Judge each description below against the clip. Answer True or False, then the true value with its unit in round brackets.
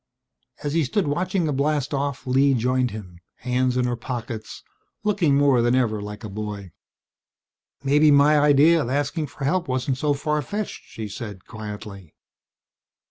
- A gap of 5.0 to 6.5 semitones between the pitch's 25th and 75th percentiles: False (4.3 semitones)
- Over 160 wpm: False (155 wpm)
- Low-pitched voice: True (130 Hz)